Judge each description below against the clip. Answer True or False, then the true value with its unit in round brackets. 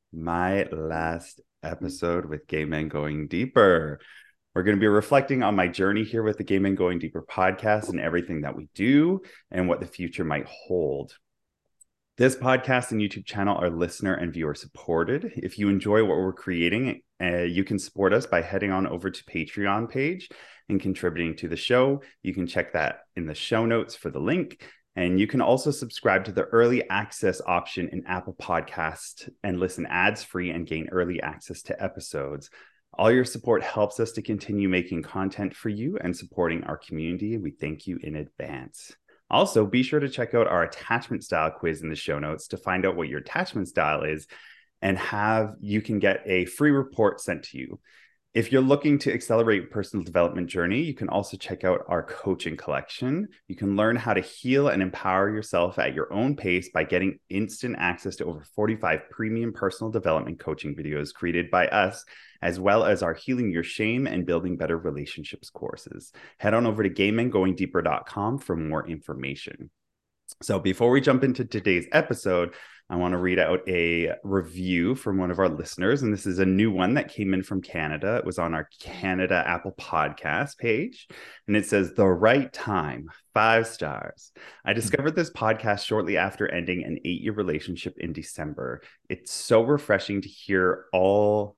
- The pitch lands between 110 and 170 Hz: False (95 Hz)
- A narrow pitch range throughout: False (4.1 semitones)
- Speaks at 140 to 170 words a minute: False (185 wpm)